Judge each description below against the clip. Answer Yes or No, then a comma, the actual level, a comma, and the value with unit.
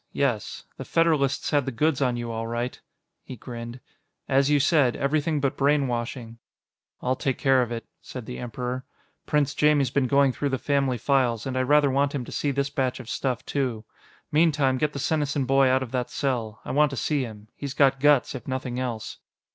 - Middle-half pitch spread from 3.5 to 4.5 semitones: No, narrow, 2.4 semitones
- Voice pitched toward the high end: No, low, 135 Hz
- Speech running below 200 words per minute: No, fast, 205 wpm